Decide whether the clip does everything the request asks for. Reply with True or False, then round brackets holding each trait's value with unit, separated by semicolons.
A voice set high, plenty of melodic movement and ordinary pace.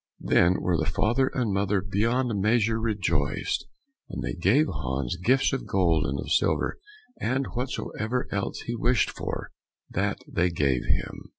False (100 Hz; 5.7 semitones; 155 wpm)